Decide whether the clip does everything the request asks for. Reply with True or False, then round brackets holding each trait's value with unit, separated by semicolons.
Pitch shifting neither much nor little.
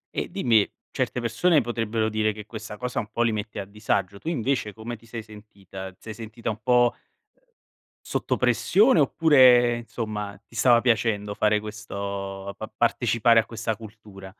False (2.3 semitones)